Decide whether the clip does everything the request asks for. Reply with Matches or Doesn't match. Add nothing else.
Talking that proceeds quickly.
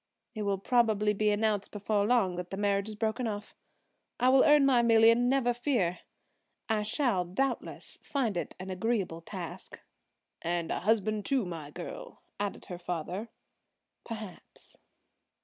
Doesn't match